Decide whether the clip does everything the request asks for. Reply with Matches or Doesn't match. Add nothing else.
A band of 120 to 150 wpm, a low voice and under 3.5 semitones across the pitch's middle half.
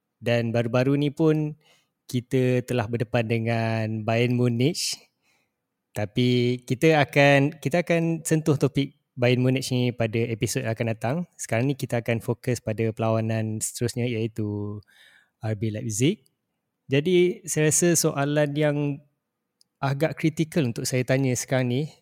Doesn't match